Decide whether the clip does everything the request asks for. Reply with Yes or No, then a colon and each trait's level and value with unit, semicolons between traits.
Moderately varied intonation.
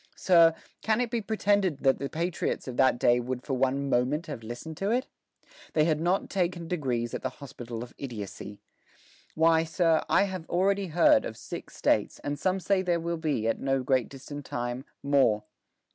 No: wide, 5.7 semitones